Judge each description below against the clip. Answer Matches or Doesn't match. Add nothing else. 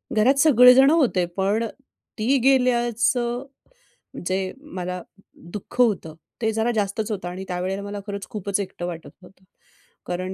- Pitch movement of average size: Matches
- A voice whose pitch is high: Matches